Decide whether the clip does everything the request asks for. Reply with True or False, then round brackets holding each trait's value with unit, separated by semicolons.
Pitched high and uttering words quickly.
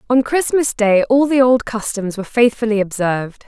False (230 Hz; 175 wpm)